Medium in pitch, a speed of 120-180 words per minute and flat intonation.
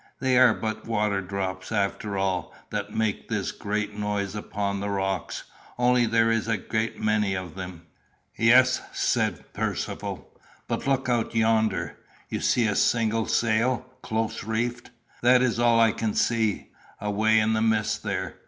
No: low, 110 Hz; average, 155 wpm; narrow, 2.1 semitones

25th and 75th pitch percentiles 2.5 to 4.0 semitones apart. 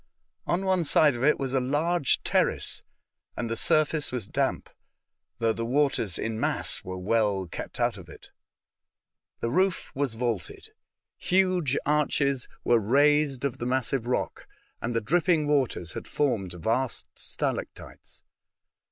No: average, 4.6 semitones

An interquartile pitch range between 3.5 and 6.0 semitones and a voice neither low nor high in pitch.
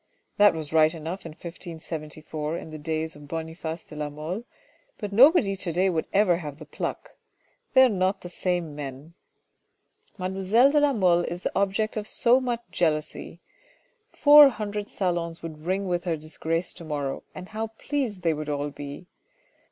Yes: average, 4.4 semitones; medium, 175 Hz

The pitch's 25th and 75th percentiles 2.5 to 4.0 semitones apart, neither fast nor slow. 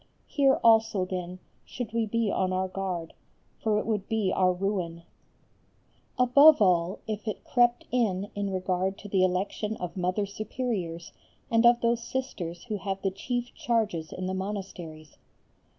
Yes: average, 3.7 semitones; average, 155 wpm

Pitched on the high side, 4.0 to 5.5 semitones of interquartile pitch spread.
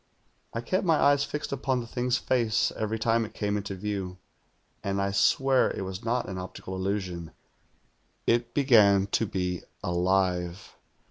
No: low, 105 Hz; average, 4.5 semitones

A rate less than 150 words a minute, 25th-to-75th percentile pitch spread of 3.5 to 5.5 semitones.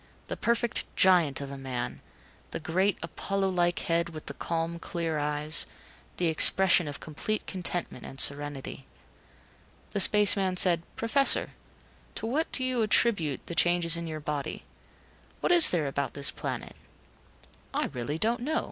No: average, 155 wpm; average, 4.9 semitones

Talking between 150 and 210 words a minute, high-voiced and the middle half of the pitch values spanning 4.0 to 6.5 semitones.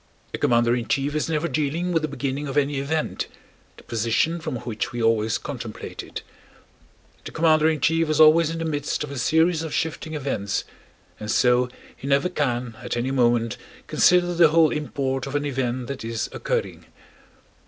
No: average, 180 wpm; medium, 140 Hz; average, 4.4 semitones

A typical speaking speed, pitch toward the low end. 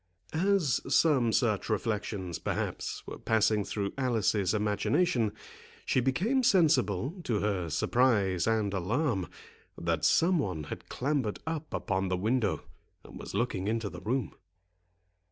No: slow, 130 wpm; low, 110 Hz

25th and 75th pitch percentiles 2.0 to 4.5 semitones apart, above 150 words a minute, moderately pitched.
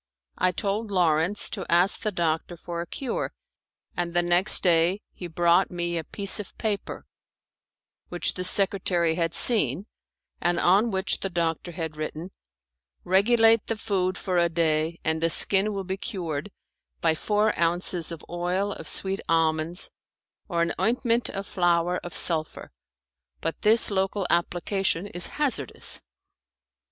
No: average, 2.9 semitones; average, 145 wpm; medium, 175 Hz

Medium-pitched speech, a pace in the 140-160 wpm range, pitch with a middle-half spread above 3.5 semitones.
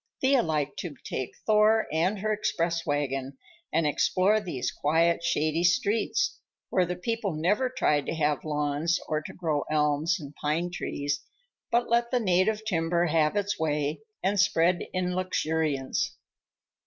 Yes: medium, 170 Hz; average, 150 wpm; average, 4.9 semitones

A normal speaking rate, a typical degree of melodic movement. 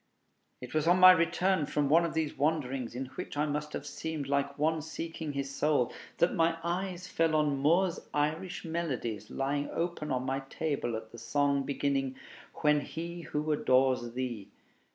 Yes: average, 175 wpm; average, 3.3 semitones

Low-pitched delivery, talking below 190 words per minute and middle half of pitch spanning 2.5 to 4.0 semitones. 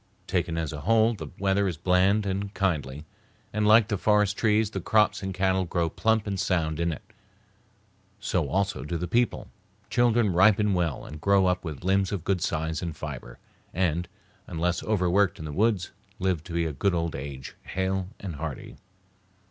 Yes: very low, 95 Hz; average, 180 wpm; average, 3.5 semitones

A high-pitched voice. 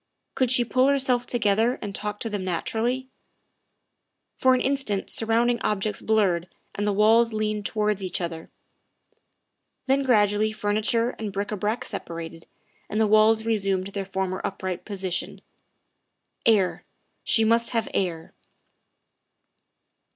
Yes: high, 215 Hz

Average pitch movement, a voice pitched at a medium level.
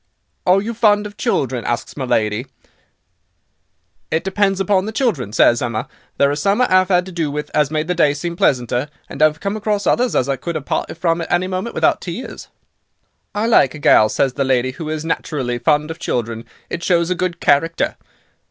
No: wide, 5.9 semitones; medium, 160 Hz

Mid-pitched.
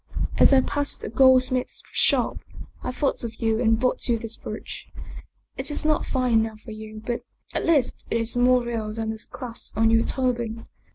No: high, 235 Hz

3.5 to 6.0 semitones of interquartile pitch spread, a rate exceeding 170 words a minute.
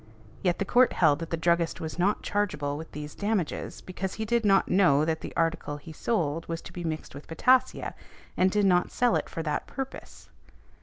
Yes: average, 4.5 semitones; fast, 205 wpm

